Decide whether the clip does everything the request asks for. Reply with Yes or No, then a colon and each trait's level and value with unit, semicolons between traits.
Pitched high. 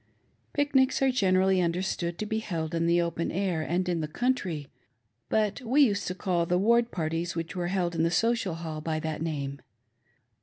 No: medium, 175 Hz